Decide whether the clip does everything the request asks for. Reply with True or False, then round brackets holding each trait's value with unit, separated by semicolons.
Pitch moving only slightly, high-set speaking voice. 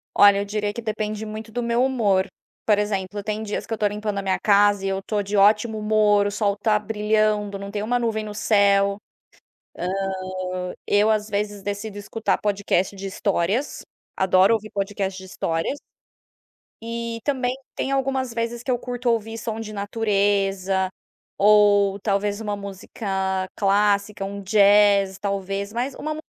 True (1.7 semitones; 205 Hz)